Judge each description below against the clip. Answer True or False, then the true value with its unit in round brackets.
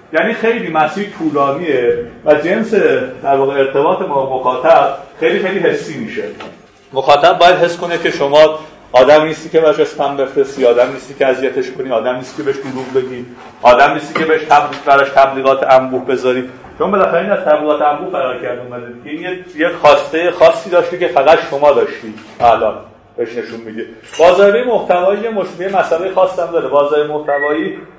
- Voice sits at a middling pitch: True (150 Hz)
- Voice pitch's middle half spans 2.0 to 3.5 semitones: False (4.6 semitones)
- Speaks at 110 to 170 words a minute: True (155 wpm)